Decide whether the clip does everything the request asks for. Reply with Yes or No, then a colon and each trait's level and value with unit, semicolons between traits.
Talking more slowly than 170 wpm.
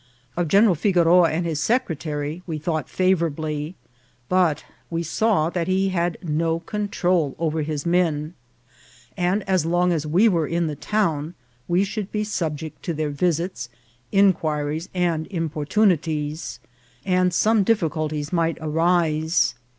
Yes: slow, 135 wpm